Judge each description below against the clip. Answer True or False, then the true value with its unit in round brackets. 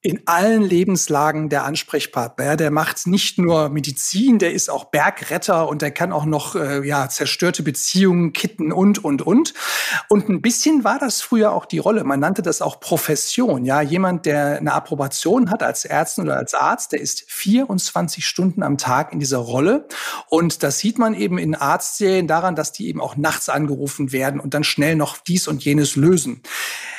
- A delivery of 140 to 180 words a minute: False (190 wpm)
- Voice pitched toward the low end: False (165 Hz)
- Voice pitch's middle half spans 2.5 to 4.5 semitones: False (5.0 semitones)